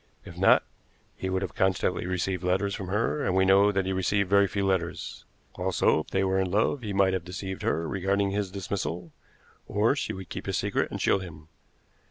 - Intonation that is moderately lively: No, narrow, 1.4 semitones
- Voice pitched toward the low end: Yes, very low, 95 Hz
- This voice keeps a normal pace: No, fast, 210 wpm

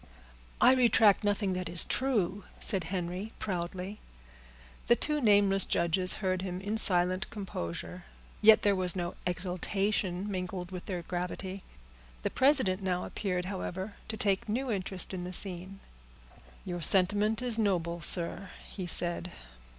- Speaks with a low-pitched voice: No, high, 190 Hz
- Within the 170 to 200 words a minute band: No, average, 140 wpm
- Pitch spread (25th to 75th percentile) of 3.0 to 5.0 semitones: No, narrow, 2.4 semitones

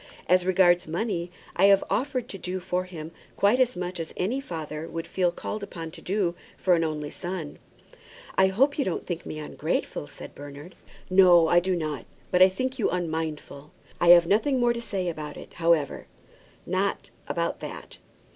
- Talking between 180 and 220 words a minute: Yes, average, 185 wpm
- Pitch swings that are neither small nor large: Yes, average, 3.1 semitones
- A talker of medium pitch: Yes, medium, 180 Hz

